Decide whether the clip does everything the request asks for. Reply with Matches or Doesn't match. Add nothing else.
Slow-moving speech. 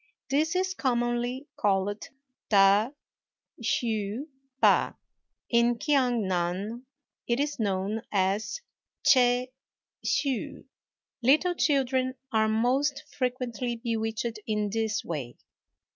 Matches